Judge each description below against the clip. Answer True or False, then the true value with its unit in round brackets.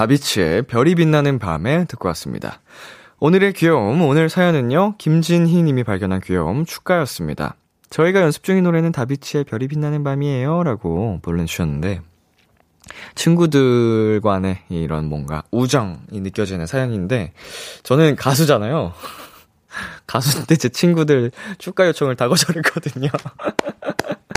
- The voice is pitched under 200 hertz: True (140 Hz)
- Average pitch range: False (8.4 semitones)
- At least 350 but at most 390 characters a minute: False (305 characters per minute)